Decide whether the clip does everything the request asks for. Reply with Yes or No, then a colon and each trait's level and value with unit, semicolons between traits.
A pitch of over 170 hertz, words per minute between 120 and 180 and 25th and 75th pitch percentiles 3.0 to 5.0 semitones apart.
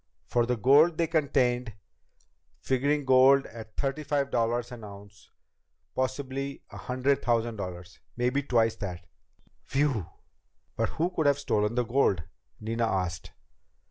No: low, 125 Hz; slow, 135 wpm; average, 3.8 semitones